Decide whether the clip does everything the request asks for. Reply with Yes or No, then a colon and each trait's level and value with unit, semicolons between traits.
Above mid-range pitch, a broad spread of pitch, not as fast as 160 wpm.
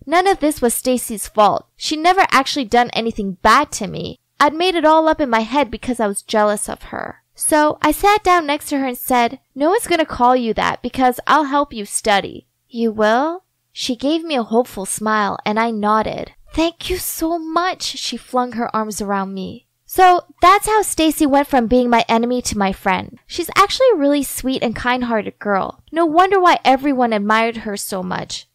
No: very high, 255 Hz; wide, 6.0 semitones; fast, 205 wpm